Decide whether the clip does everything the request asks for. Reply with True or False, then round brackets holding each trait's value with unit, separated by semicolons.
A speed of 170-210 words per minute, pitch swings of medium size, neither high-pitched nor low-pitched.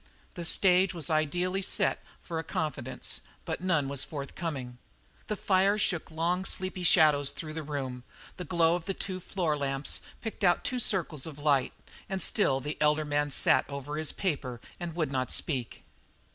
True (175 wpm; 4.2 semitones; 155 Hz)